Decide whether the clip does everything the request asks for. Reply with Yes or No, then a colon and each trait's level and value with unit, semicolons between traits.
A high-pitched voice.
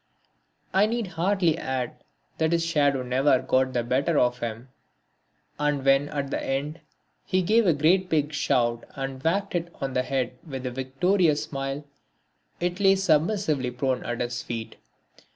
No: medium, 140 Hz